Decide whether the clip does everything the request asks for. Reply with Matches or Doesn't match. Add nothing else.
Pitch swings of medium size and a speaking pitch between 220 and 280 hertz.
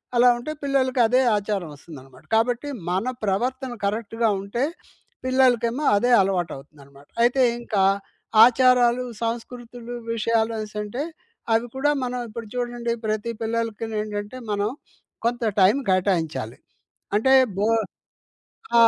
Matches